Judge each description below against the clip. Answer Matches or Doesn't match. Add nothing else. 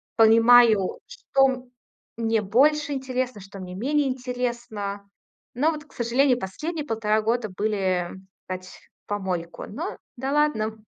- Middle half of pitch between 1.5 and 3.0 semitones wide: Doesn't match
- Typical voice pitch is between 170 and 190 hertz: Doesn't match